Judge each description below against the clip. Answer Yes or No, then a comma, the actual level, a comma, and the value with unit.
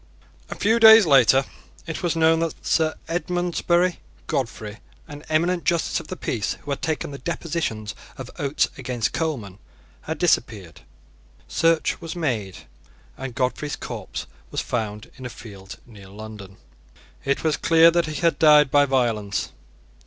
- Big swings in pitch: Yes, wide, 6.7 semitones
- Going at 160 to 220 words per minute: No, average, 150 wpm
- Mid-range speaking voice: Yes, medium, 145 Hz